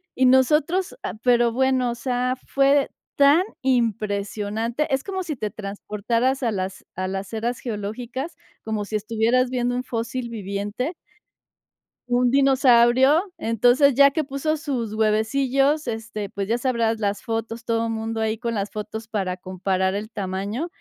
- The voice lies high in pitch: Yes, high, 235 Hz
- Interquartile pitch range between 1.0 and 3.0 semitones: No, average, 3.6 semitones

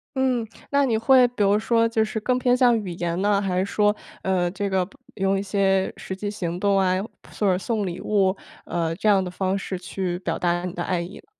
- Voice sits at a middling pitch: No, high, 195 Hz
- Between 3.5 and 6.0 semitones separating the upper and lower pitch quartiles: No, average, 3.1 semitones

